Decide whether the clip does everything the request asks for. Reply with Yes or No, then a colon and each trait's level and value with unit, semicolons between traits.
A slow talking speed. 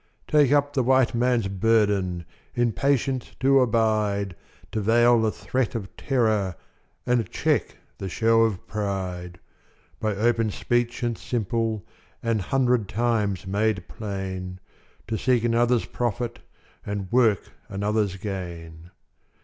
Yes: slow, 125 wpm